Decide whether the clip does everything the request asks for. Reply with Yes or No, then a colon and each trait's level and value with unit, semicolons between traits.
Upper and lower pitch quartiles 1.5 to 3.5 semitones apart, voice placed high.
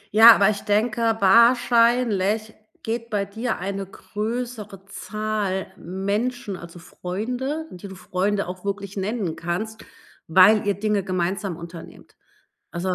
Yes: average, 2.9 semitones; high, 205 Hz